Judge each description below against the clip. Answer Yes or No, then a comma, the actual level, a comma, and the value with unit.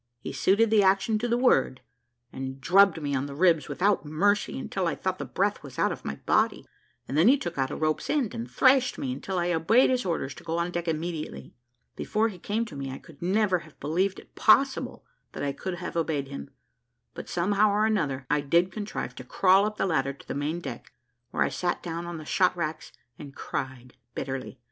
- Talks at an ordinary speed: No, fast, 220 wpm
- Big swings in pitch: Yes, wide, 6.1 semitones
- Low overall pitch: No, medium, 170 Hz